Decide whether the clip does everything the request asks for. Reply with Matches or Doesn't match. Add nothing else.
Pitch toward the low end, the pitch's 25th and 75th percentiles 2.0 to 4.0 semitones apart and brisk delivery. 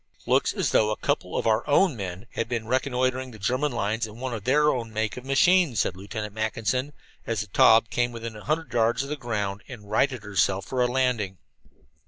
Matches